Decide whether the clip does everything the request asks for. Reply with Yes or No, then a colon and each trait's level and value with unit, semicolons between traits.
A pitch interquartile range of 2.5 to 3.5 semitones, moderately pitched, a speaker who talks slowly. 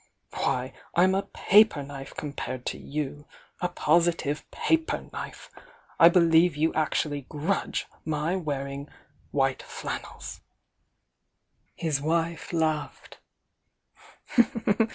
Yes: average, 3.0 semitones; medium, 155 Hz; slow, 100 wpm